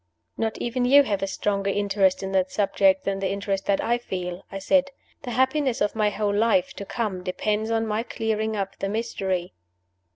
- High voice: Yes, high, 205 Hz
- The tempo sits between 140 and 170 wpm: No, average, 195 wpm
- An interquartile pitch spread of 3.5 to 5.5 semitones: No, average, 2.7 semitones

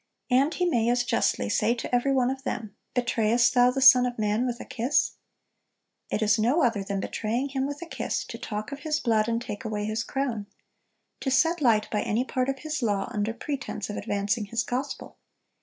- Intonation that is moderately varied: Yes, average, 3.8 semitones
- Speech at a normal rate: No, fast, 210 wpm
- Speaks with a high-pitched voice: Yes, high, 245 Hz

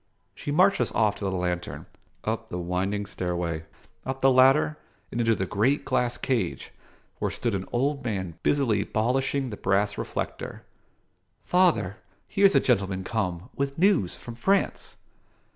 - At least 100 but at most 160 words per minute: Yes, average, 150 wpm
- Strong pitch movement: Yes, wide, 6.1 semitones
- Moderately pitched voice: No, low, 115 Hz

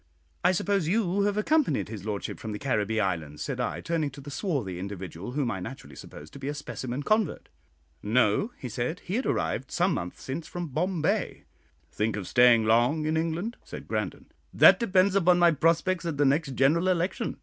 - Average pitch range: No, wide, 8.0 semitones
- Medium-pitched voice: Yes, medium, 145 Hz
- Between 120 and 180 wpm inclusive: No, average, 195 wpm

